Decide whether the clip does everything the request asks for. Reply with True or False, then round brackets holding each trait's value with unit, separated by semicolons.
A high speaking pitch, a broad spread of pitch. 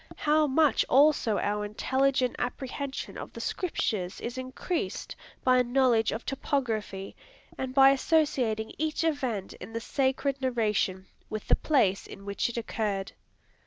False (255 Hz; 4.2 semitones)